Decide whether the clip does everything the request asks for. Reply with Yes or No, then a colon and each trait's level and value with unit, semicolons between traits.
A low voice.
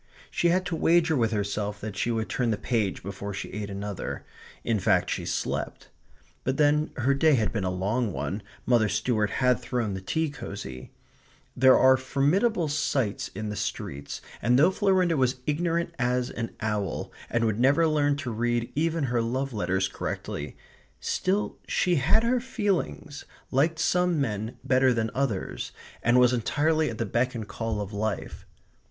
Yes: low, 125 Hz